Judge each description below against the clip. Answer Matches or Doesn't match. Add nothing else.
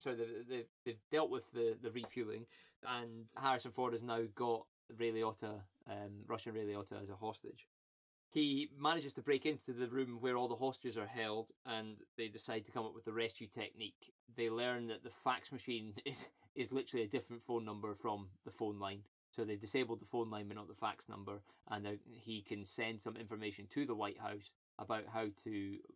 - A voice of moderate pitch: Doesn't match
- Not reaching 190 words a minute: Doesn't match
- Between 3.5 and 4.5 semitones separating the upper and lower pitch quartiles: Doesn't match